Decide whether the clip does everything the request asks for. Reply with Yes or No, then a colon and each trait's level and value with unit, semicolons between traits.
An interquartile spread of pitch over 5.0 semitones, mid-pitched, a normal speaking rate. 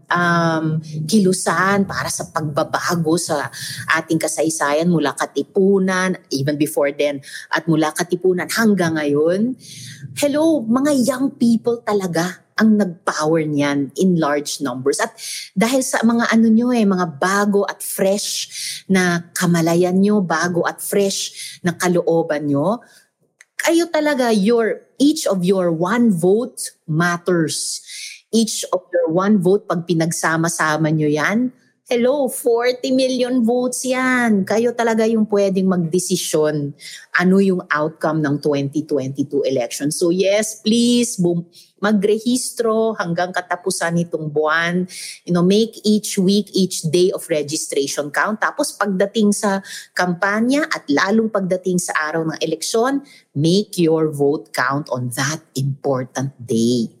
Yes: wide, 5.6 semitones; medium, 180 Hz; average, 125 wpm